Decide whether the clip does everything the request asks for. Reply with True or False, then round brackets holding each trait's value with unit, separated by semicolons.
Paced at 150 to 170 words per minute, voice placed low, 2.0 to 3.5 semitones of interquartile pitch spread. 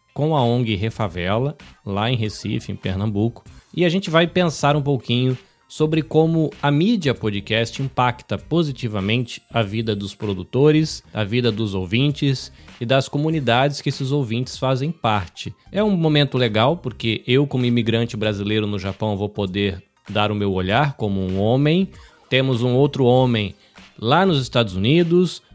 False (155 wpm; 120 Hz; 5.1 semitones)